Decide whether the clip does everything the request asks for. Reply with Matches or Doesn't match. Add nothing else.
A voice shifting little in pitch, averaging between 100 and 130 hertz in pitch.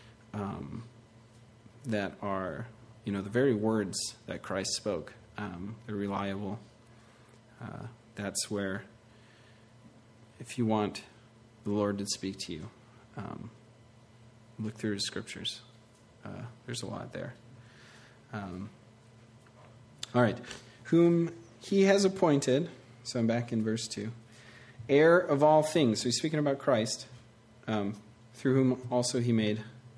Matches